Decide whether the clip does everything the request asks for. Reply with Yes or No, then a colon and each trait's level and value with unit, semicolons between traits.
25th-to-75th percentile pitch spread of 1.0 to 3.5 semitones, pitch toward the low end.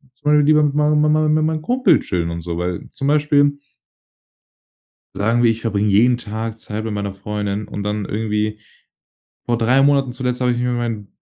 No: wide, 5.5 semitones; low, 120 Hz